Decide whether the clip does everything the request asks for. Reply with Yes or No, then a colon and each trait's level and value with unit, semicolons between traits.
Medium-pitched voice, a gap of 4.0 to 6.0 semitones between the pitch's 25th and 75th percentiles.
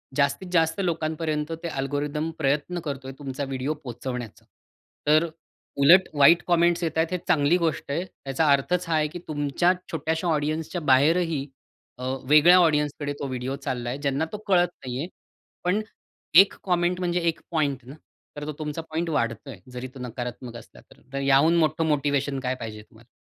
No: medium, 150 Hz; average, 3.5 semitones